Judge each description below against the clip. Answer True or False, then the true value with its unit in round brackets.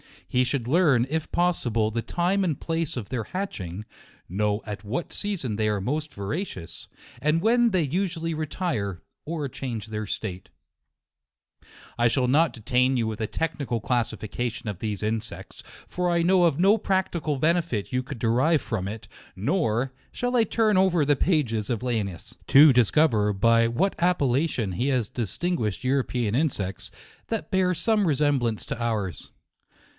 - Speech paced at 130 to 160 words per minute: False (170 wpm)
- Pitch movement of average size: False (7.3 semitones)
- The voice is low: True (130 Hz)